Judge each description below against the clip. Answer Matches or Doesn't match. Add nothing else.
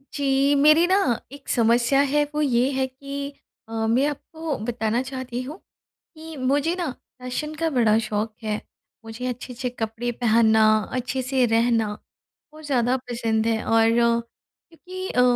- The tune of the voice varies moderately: Matches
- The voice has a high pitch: Matches